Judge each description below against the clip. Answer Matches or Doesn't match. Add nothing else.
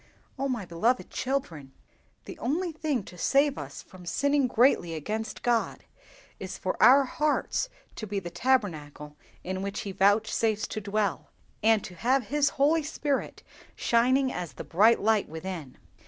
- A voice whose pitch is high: Matches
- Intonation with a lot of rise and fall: Matches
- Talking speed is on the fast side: Doesn't match